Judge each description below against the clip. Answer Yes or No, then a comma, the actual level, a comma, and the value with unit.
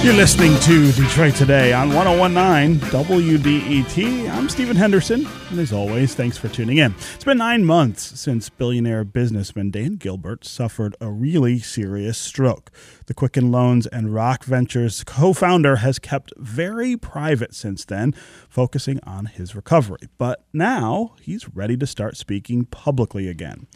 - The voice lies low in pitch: Yes, low, 130 Hz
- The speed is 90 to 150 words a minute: Yes, average, 145 wpm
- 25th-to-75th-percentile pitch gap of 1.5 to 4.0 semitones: No, wide, 5.6 semitones